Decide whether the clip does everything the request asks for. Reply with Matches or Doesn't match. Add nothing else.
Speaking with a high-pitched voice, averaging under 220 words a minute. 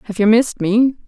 Doesn't match